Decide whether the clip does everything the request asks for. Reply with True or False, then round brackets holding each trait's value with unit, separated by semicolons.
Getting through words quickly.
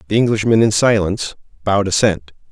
False (145 wpm)